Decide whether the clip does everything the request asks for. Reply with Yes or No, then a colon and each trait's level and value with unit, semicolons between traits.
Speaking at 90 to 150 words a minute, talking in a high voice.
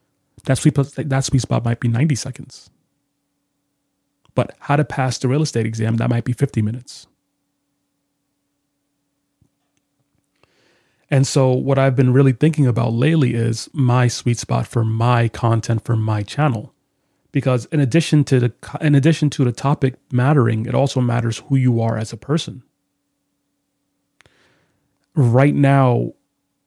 No: average, 140 wpm; low, 135 Hz